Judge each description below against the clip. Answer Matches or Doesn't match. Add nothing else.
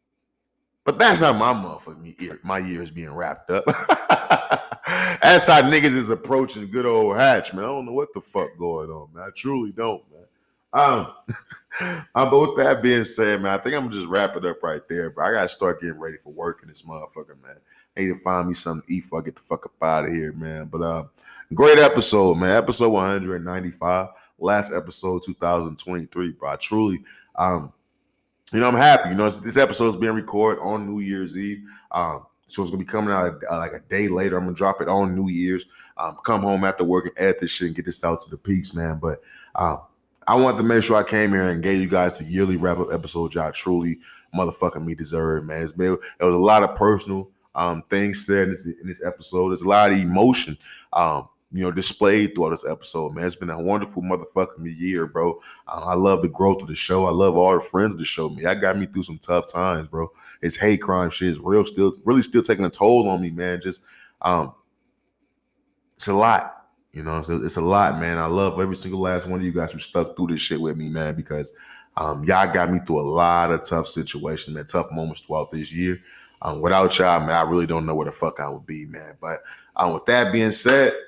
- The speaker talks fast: Matches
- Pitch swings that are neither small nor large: Matches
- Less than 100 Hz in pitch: Matches